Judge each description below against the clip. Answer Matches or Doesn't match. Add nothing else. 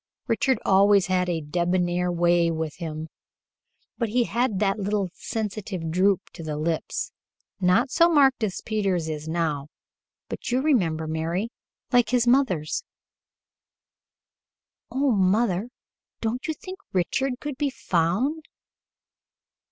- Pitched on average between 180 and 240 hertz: Matches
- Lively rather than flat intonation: Matches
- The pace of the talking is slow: Matches